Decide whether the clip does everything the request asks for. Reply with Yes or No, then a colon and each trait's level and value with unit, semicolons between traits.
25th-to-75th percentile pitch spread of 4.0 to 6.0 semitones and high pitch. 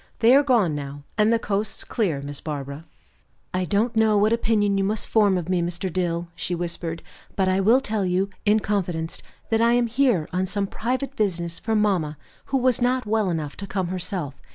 Yes: average, 4.4 semitones; high, 195 Hz